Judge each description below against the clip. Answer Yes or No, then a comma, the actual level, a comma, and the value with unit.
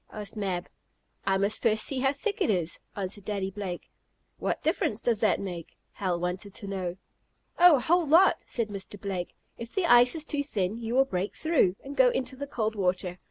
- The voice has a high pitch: Yes, high, 210 Hz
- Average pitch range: No, wide, 6.1 semitones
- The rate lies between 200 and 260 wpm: Yes, fast, 205 wpm